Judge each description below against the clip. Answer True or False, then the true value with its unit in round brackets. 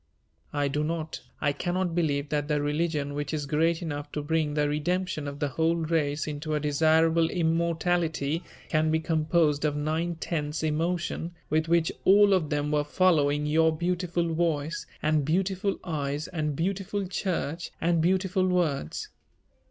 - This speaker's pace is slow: False (155 wpm)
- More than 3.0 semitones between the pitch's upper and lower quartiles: False (2.6 semitones)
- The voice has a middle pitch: True (160 Hz)